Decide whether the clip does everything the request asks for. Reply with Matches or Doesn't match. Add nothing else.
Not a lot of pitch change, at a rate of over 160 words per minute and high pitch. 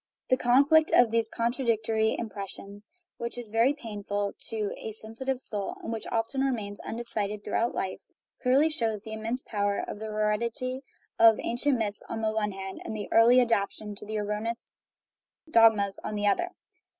Matches